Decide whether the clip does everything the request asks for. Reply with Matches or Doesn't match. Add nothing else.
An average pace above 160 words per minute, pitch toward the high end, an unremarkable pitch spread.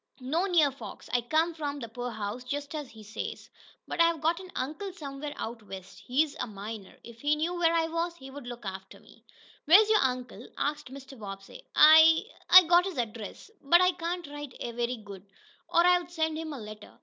Doesn't match